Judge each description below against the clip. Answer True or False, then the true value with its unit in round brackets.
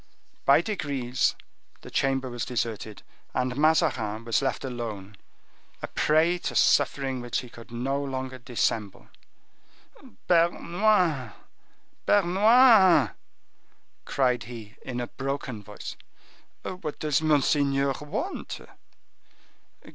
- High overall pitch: False (135 Hz)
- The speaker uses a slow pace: True (100 wpm)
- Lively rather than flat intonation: False (4.6 semitones)